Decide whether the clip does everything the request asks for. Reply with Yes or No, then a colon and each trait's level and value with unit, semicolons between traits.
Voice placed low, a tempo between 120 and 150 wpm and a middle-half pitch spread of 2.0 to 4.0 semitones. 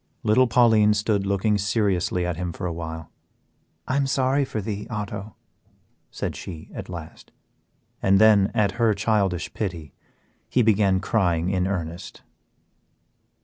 Yes: low, 100 Hz; average, 140 wpm; average, 3.4 semitones